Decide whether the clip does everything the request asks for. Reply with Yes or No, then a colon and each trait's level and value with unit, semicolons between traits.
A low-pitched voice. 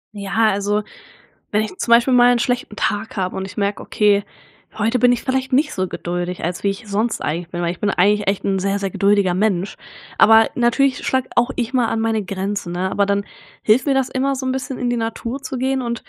No: high, 215 Hz